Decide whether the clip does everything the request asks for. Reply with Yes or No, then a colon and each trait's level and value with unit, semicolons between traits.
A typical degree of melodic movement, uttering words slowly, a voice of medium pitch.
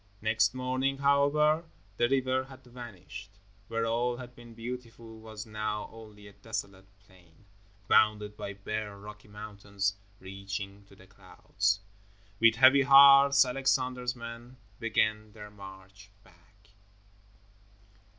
No: average, 3.9 semitones; slow, 120 wpm; low, 110 Hz